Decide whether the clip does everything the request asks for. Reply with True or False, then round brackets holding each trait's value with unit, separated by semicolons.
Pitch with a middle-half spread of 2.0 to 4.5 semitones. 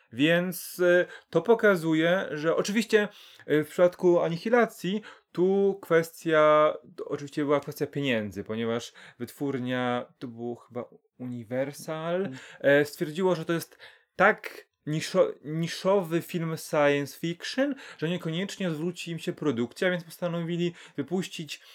True (3.7 semitones)